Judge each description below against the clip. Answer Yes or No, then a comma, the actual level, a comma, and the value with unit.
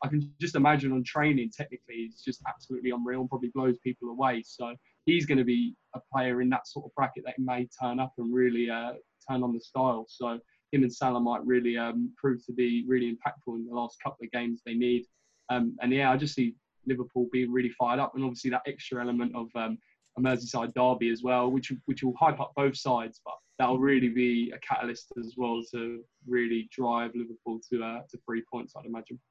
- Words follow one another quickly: Yes, fast, 225 wpm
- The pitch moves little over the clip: Yes, narrow, 1.6 semitones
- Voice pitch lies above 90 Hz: Yes, low, 125 Hz